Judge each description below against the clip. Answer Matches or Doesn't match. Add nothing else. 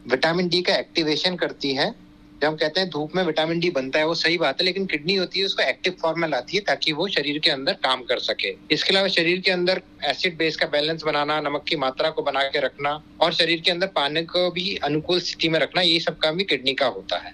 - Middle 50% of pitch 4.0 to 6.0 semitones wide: Doesn't match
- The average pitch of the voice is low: Doesn't match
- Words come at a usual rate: Doesn't match